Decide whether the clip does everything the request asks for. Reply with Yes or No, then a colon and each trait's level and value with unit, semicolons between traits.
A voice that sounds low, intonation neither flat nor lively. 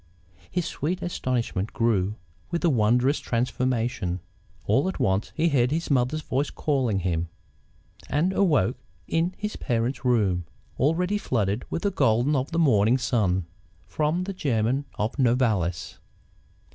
No: low, 125 Hz; wide, 6.0 semitones